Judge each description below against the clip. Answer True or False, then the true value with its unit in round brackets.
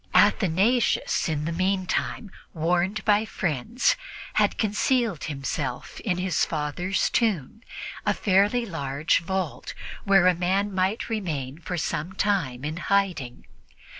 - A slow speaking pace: True (120 wpm)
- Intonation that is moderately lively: True (4.4 semitones)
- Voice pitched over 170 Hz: True (185 Hz)